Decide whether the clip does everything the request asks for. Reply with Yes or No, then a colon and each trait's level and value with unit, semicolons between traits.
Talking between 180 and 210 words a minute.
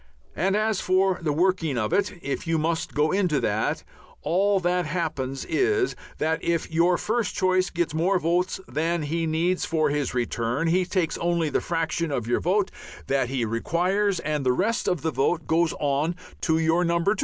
Yes: average, 190 wpm